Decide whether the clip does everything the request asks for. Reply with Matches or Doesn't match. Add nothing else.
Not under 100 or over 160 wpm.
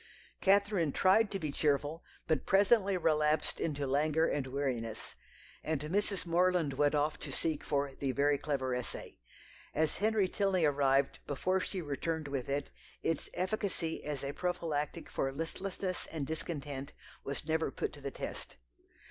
Matches